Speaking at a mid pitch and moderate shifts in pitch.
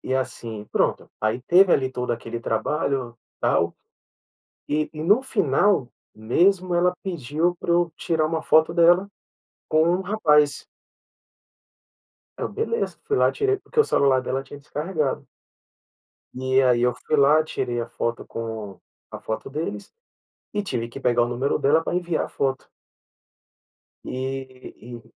No: medium, 145 Hz; wide, 5.9 semitones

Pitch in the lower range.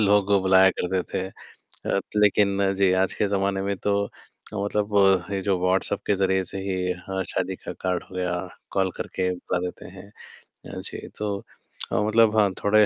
Yes: very low, 95 Hz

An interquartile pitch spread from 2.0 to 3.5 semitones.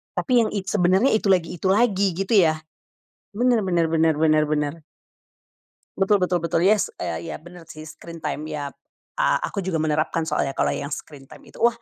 No: average, 4.2 semitones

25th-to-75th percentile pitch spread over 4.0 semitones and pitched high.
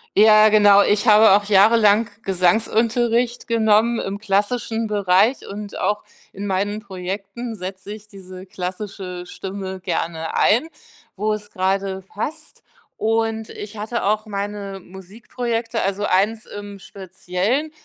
No: narrow, 2.5 semitones; high, 205 Hz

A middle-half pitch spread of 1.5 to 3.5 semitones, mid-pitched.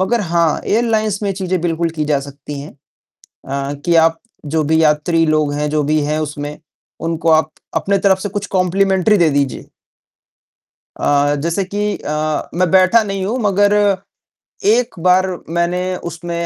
No: average, 4.2 semitones; medium, 170 Hz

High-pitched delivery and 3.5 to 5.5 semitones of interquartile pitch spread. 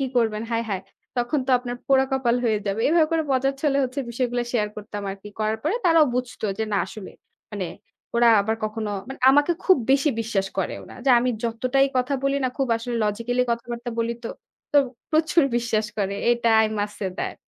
Yes: high, 240 Hz; average, 3.8 semitones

